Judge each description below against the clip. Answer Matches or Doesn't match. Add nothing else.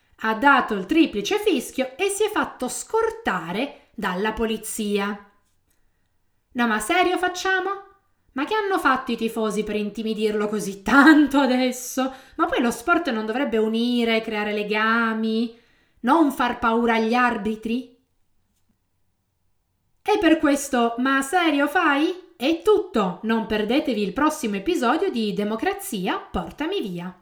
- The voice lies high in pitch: Matches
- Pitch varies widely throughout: Matches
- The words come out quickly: Doesn't match